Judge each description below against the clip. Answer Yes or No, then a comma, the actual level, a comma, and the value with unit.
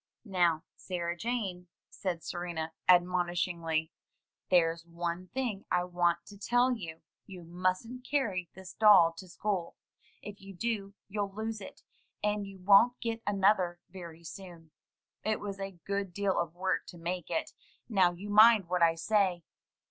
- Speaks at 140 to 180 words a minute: Yes, average, 150 wpm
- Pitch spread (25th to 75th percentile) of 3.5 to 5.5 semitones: No, average, 3.0 semitones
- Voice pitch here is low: No, medium, 185 Hz